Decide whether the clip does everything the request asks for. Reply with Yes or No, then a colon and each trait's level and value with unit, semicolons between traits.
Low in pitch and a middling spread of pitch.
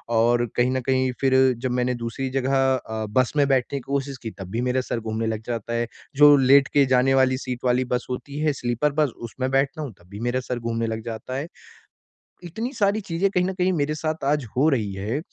Yes: low, 130 Hz; average, 3.3 semitones